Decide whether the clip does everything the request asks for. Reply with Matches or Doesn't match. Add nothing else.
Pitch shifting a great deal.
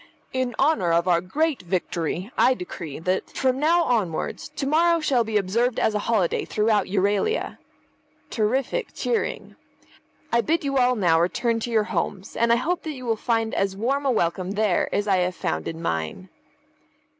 Matches